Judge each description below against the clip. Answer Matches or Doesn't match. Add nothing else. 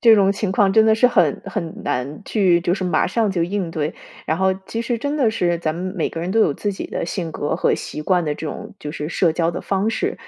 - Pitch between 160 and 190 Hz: Matches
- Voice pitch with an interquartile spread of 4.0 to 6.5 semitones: Matches